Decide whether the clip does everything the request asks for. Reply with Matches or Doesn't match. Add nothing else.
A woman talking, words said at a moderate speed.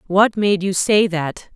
Matches